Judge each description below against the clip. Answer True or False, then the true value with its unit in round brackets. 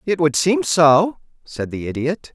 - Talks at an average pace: True (180 wpm)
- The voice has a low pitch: False (160 Hz)